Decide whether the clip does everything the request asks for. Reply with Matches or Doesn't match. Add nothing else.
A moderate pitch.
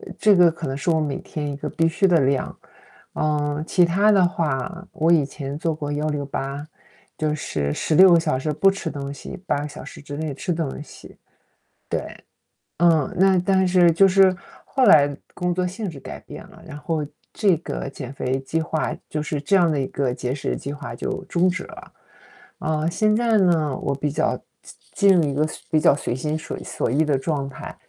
Matches